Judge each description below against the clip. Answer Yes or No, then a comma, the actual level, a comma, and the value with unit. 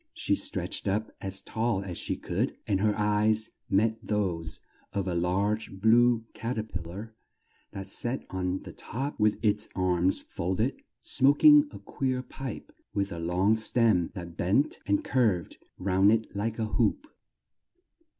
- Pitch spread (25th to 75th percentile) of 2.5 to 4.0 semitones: Yes, average, 3.2 semitones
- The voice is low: Yes, low, 105 Hz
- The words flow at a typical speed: Yes, average, 160 wpm